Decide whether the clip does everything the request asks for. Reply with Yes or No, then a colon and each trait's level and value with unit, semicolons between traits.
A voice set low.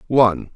Yes: low, 105 Hz